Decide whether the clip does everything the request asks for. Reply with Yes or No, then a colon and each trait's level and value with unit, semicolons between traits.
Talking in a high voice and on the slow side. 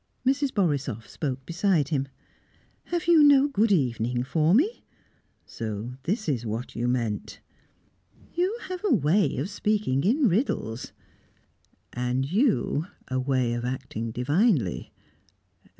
No: medium, 145 Hz; slow, 125 wpm